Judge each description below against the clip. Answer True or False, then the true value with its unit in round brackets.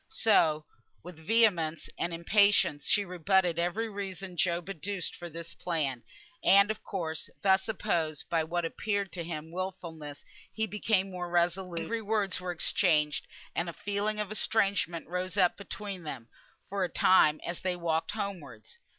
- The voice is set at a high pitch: False (180 Hz)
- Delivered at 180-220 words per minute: False (160 wpm)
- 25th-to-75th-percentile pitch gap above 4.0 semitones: False (3.3 semitones)